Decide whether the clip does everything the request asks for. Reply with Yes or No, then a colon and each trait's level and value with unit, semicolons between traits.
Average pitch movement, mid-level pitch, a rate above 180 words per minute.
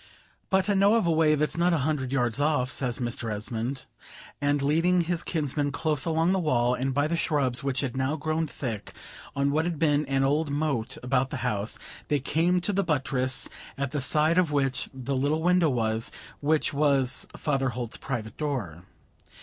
Yes: average, 3.5 semitones; medium, 145 Hz; average, 190 wpm